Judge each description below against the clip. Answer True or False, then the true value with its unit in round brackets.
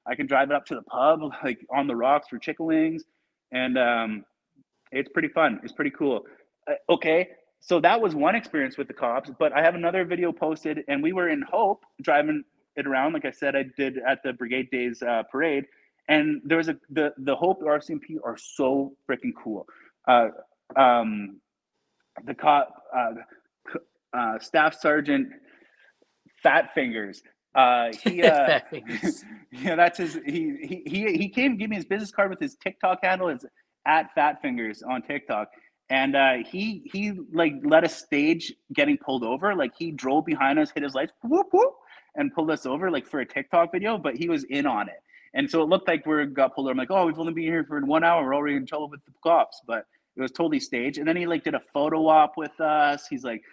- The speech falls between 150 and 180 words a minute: False (205 wpm)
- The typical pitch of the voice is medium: True (160 Hz)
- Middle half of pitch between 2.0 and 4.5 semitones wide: False (5.3 semitones)